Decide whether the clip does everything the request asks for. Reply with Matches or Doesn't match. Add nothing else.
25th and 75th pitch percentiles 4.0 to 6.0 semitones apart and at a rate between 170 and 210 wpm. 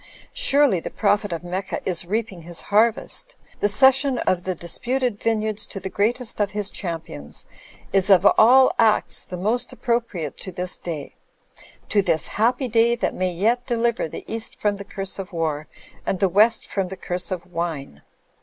Matches